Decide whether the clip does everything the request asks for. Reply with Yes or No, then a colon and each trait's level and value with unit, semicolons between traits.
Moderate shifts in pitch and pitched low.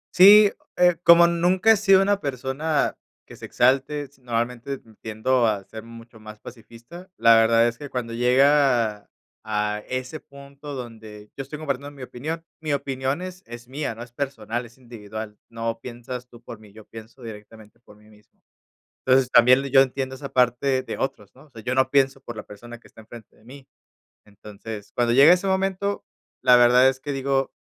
Yes: average, 3.5 semitones; low, 125 Hz